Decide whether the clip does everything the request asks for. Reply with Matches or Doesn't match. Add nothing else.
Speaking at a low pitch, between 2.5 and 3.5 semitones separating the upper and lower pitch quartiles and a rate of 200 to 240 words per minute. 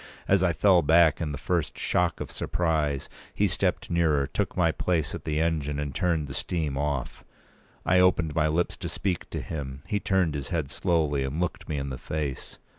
Matches